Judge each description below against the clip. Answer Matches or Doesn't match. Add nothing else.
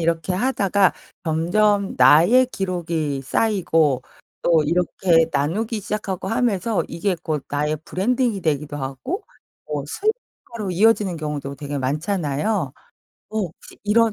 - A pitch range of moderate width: Doesn't match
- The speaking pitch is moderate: Matches